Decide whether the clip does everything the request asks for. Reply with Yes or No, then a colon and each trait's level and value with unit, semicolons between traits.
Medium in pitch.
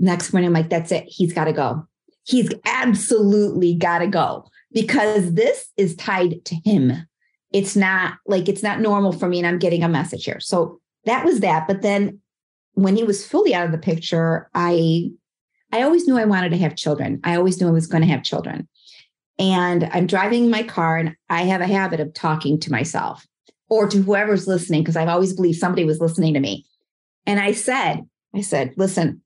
Yes: medium, 180 Hz